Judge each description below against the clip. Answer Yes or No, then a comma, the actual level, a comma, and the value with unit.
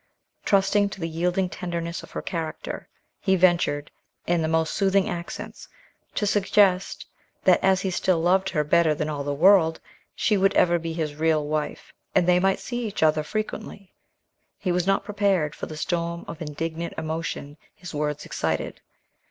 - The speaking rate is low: No, average, 170 wpm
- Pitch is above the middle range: No, medium, 170 Hz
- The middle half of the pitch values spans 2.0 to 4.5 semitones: Yes, average, 3.3 semitones